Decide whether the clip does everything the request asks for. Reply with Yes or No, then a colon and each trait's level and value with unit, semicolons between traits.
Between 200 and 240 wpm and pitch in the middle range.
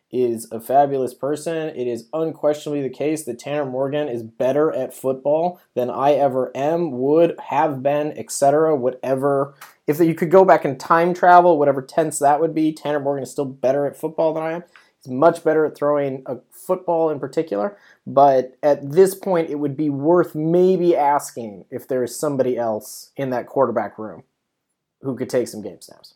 No: average, 190 wpm; medium, 145 Hz